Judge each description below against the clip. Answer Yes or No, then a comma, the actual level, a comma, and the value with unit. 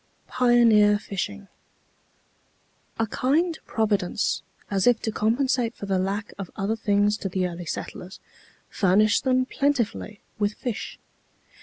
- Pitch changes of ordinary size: Yes, average, 3.3 semitones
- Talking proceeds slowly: Yes, slow, 125 wpm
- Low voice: No, high, 210 Hz